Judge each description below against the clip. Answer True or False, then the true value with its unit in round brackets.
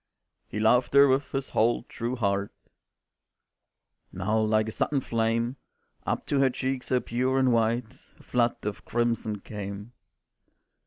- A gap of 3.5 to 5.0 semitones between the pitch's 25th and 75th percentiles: False (2.9 semitones)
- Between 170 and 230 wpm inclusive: False (145 wpm)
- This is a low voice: True (115 Hz)